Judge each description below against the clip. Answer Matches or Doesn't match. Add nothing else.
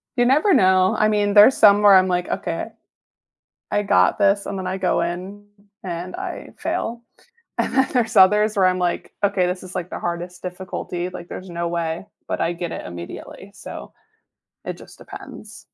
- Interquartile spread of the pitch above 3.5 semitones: Doesn't match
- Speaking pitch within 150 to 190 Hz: Matches